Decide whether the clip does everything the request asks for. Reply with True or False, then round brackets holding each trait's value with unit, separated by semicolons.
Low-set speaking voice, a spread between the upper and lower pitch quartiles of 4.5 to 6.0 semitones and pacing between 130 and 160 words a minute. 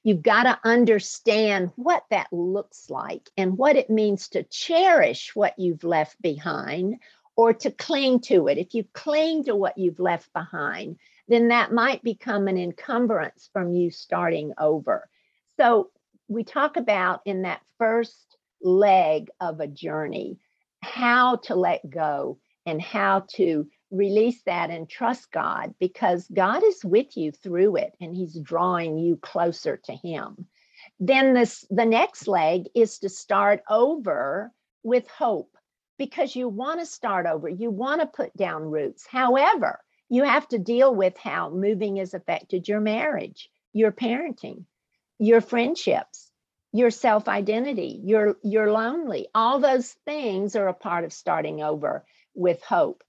False (215 Hz; 5.4 semitones; 150 wpm)